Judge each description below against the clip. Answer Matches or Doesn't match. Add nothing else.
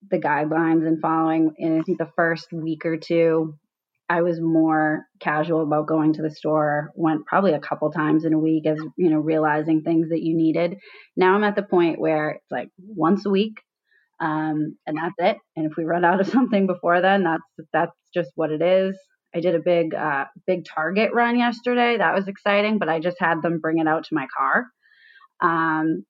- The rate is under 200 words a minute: Doesn't match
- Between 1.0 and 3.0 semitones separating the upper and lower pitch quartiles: Matches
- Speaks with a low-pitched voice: Doesn't match